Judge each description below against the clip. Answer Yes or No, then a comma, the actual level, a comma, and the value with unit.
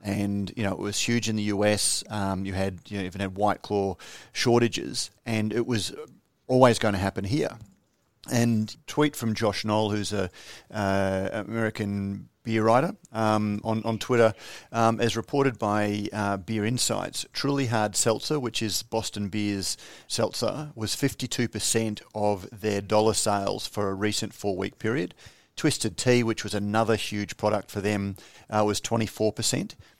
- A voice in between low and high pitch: No, low, 105 Hz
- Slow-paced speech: No, average, 160 wpm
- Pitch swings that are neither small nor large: No, narrow, 2.1 semitones